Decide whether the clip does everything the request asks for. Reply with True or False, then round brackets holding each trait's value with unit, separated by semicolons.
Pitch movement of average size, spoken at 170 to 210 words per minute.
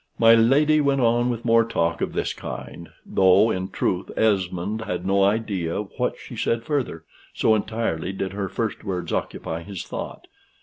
True (3.7 semitones; 175 wpm)